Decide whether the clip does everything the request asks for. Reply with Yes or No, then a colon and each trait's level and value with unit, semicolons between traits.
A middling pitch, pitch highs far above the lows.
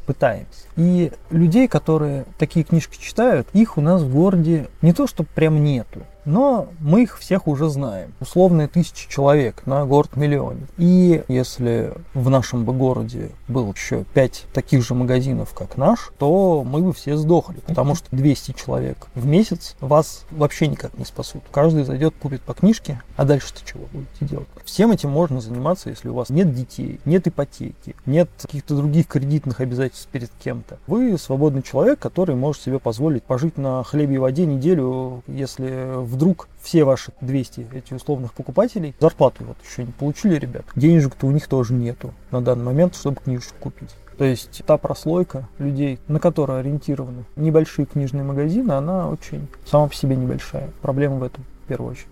No: medium, 145 Hz; average, 4.0 semitones